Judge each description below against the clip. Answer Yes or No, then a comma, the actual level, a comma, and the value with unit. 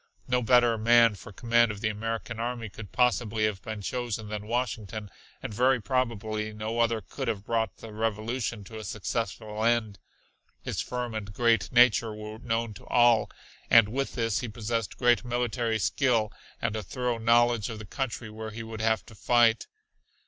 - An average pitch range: No, narrow, 1.8 semitones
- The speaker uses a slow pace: No, average, 180 wpm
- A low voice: Yes, low, 115 Hz